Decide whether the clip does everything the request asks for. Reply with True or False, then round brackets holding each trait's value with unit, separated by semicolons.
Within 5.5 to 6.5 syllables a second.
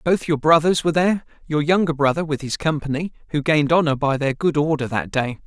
True (6.1 syllables/s)